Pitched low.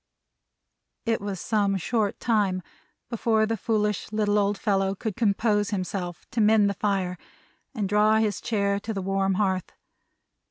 No: high, 205 Hz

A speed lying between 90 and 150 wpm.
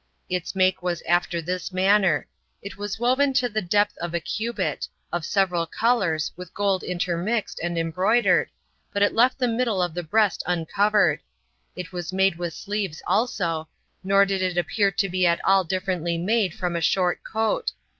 No: average, 175 wpm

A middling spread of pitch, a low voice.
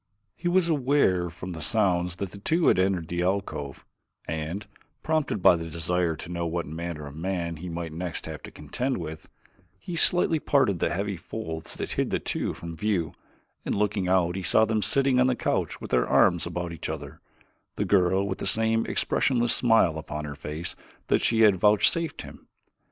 Yes: average, 5.0 semitones; very low, 90 Hz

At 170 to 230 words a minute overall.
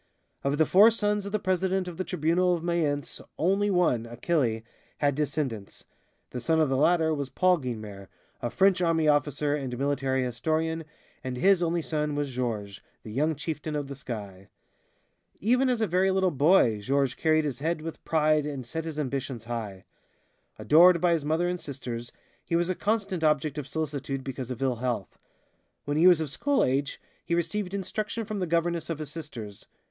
Yes: average, 185 wpm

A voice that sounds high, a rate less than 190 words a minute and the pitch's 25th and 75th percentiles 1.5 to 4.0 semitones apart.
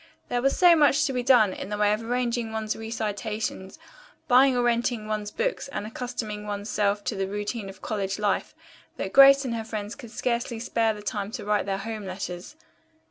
No: high, 220 Hz; average, 200 wpm; average, 2.9 semitones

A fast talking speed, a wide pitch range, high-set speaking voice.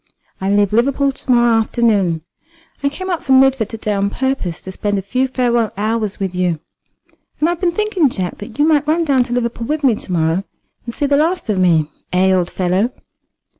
Yes: fast, 215 wpm; wide, 6.1 semitones; high, 230 Hz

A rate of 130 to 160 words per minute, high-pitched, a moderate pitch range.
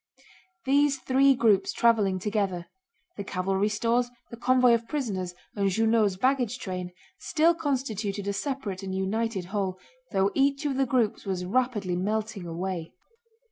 Yes: slow, 135 wpm; high, 215 Hz; average, 5.0 semitones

